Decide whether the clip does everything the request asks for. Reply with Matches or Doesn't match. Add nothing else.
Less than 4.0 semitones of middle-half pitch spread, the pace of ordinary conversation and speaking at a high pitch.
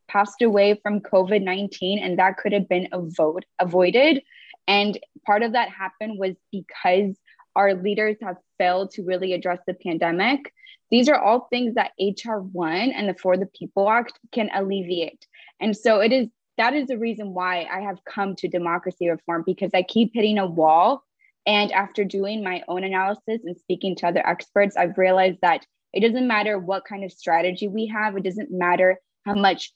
Matches